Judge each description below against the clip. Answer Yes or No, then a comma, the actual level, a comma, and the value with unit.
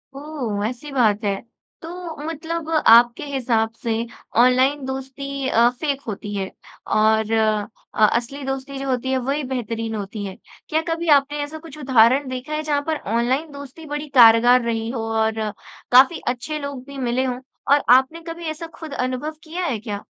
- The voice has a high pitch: Yes, very high, 260 Hz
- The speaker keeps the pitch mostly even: No, average, 4.1 semitones